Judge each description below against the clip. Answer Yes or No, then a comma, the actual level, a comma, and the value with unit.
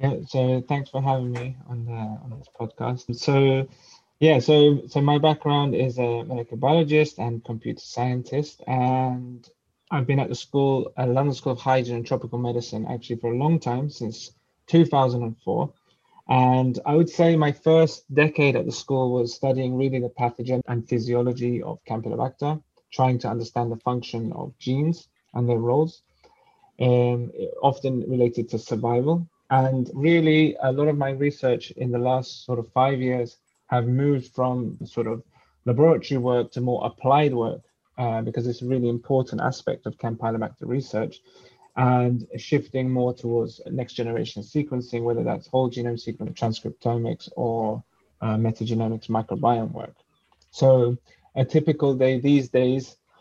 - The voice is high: No, low, 125 Hz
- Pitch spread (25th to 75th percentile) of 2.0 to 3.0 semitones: Yes, narrow, 2.6 semitones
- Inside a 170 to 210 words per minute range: No, average, 155 wpm